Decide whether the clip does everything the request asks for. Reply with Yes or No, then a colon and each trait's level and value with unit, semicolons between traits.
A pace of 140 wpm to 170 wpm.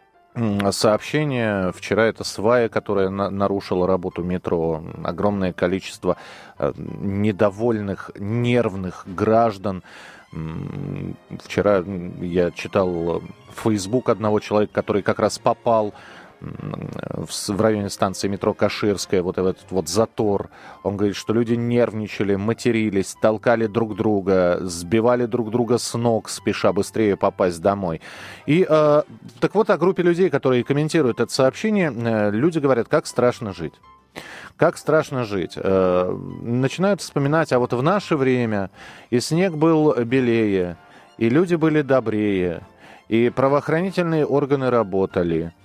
No: average, 120 wpm